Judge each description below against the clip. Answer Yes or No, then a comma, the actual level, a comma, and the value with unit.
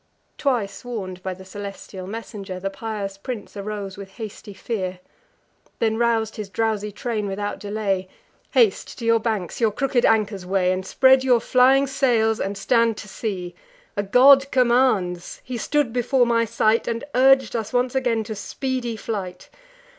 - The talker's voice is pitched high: Yes, high, 220 Hz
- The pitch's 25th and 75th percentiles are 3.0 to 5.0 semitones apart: Yes, average, 3.7 semitones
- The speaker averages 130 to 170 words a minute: Yes, average, 160 wpm